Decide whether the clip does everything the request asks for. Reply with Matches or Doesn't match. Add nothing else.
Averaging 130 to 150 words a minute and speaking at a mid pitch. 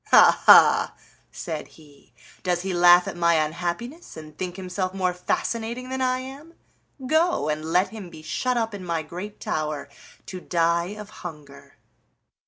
Doesn't match